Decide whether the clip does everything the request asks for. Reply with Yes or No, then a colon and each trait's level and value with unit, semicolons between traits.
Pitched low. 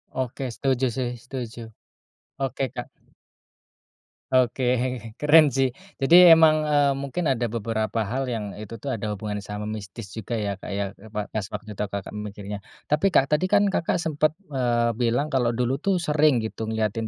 Yes: low, 120 Hz